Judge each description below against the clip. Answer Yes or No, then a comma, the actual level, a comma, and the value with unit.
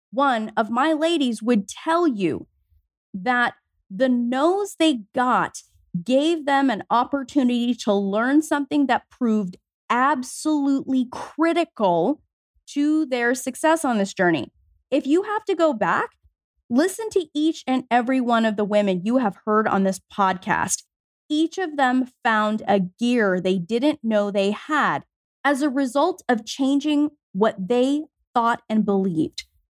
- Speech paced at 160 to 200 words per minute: No, average, 145 wpm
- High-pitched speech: Yes, very high, 250 Hz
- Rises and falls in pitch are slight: No, wide, 5.6 semitones